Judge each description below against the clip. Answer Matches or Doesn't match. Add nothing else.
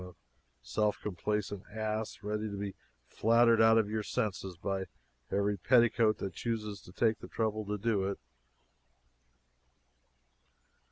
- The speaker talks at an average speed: Doesn't match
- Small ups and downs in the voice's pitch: Matches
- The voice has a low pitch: Matches